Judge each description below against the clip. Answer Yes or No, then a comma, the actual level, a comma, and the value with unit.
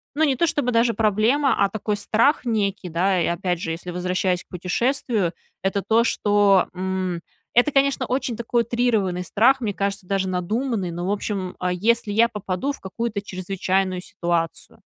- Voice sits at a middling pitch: No, high, 200 Hz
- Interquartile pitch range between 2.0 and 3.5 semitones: No, average, 4.3 semitones